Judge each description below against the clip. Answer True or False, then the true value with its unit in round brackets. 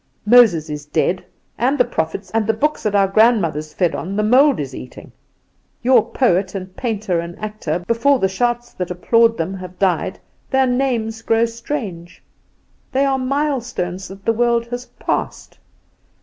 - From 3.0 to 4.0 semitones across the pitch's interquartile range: False (5.0 semitones)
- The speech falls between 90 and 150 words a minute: False (165 wpm)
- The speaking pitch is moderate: False (215 Hz)